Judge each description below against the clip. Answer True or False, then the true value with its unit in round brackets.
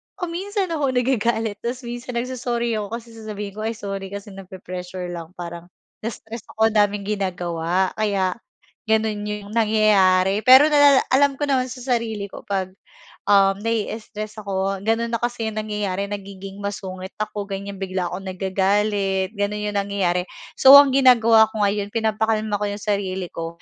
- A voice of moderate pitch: False (210 Hz)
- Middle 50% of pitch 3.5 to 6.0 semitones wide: False (2.9 semitones)